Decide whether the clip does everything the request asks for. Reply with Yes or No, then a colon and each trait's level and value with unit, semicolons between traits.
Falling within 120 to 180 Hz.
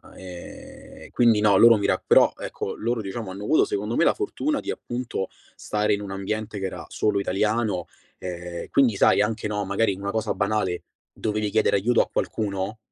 No: low, 105 Hz